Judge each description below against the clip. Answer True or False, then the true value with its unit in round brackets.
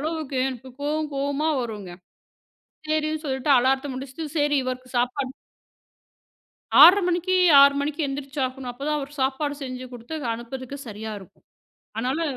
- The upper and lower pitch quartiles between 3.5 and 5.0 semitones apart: False (2.9 semitones)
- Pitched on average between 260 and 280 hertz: True (275 Hz)